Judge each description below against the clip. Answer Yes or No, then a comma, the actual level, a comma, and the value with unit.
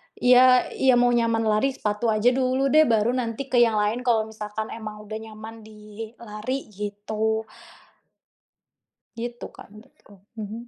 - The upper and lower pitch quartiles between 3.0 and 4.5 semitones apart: No, narrow, 2.5 semitones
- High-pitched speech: Yes, high, 225 Hz